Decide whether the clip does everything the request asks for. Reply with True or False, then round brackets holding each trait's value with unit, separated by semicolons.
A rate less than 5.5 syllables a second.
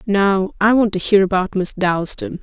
True (4.4 syllables/s)